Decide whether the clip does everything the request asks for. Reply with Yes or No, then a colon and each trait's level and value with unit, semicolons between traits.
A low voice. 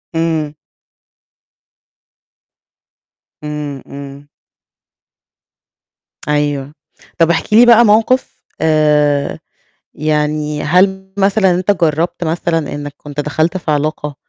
No: medium, 155 Hz